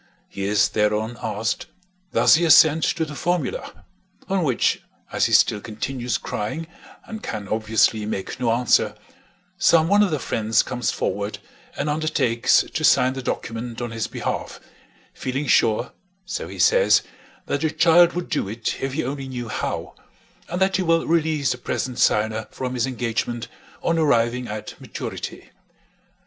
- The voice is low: Yes, low, 125 Hz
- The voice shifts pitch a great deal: Yes, wide, 6.0 semitones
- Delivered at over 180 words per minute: No, average, 160 wpm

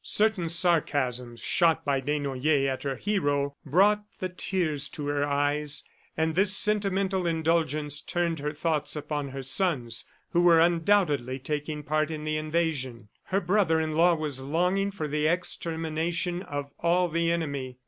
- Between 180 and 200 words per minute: No, average, 150 wpm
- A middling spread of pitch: Yes, average, 3.3 semitones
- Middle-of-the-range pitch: Yes, medium, 155 Hz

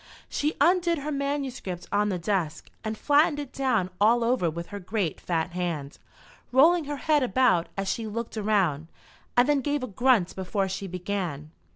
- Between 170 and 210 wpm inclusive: Yes, average, 175 wpm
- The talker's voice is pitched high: Yes, high, 215 Hz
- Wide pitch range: Yes, wide, 7.2 semitones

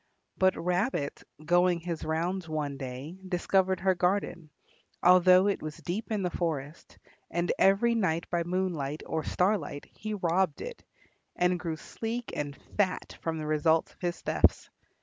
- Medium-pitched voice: Yes, medium, 175 Hz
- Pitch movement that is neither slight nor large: Yes, average, 3.0 semitones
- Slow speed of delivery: No, average, 150 wpm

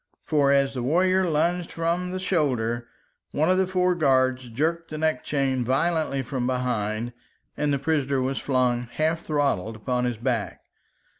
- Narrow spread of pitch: No, average, 4.7 semitones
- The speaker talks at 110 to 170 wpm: Yes, average, 160 wpm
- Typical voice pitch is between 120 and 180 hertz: Yes, medium, 140 Hz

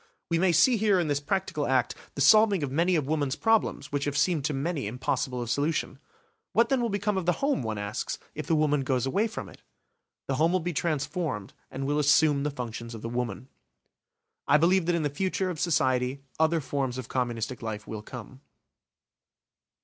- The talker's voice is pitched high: No, medium, 145 Hz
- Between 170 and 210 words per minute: Yes, fast, 205 wpm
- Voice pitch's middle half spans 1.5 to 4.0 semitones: No, average, 5.2 semitones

